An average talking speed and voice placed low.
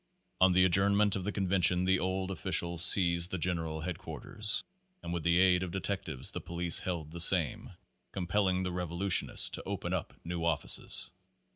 Yes: average, 170 wpm; very low, 90 Hz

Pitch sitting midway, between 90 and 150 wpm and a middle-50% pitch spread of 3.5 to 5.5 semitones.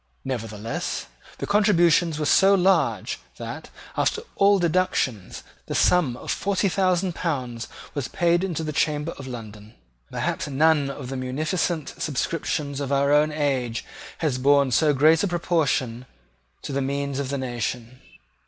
Yes: medium, 145 Hz; average, 145 wpm; average, 4.9 semitones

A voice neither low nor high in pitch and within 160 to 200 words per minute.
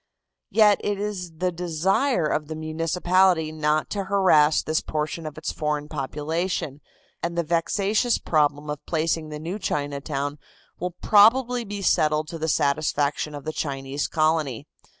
No: medium, 160 Hz; average, 150 wpm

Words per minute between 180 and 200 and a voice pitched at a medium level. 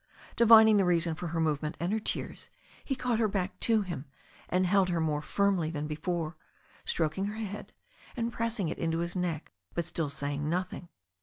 Yes: average, 190 wpm; medium, 175 Hz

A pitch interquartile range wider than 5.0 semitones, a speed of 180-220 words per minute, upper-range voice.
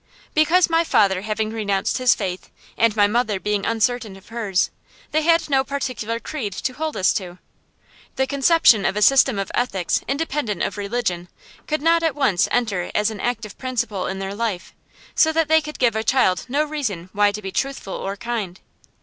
Yes: wide, 5.5 semitones; average, 190 wpm; high, 225 Hz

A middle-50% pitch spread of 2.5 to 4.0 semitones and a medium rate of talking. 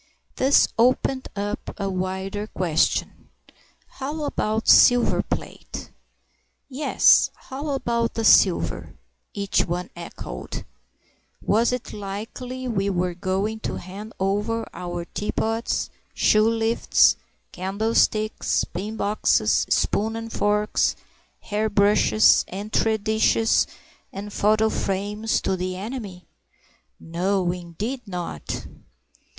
No: average, 2.9 semitones; slow, 100 wpm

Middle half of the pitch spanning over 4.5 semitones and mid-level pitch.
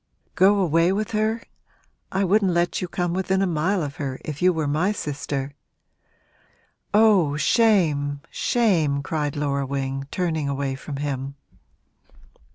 Yes: average, 5.1 semitones; medium, 160 Hz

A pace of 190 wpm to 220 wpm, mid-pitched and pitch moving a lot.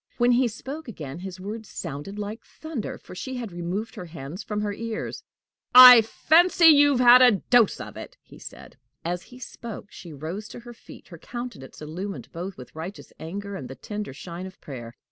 No: average, 195 wpm; high, 205 Hz; wide, 5.8 semitones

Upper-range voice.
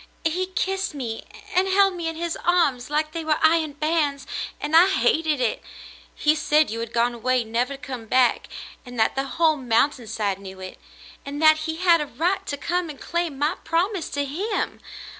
Yes: very high, 300 Hz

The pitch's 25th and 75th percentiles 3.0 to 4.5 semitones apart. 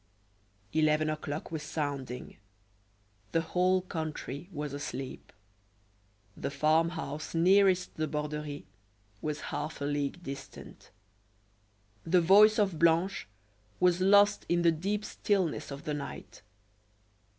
Yes: average, 3.5 semitones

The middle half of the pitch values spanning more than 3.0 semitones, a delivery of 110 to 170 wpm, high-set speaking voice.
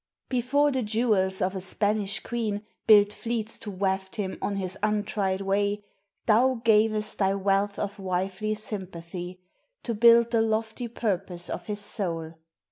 No: narrow, 2.6 semitones; average, 145 wpm; high, 205 Hz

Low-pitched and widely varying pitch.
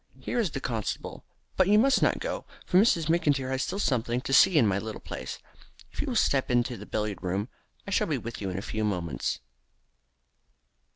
Yes: low, 125 Hz; wide, 7.4 semitones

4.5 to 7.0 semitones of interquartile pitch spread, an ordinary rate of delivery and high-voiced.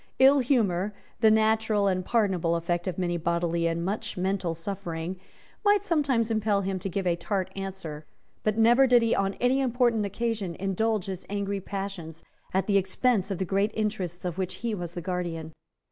No: average, 3.8 semitones; average, 180 wpm; high, 195 Hz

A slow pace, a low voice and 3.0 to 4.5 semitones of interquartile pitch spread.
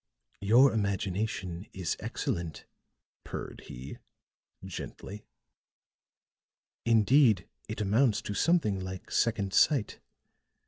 Yes: slow, 85 wpm; low, 100 Hz; average, 3.3 semitones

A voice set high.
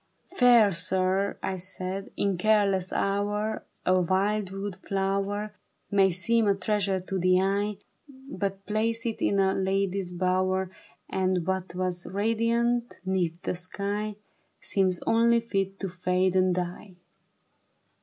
Yes: high, 195 Hz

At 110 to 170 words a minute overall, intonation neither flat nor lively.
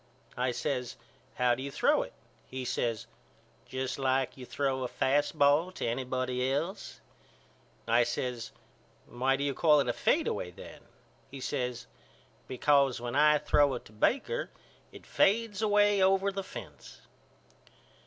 Yes: average, 145 wpm; average, 3.3 semitones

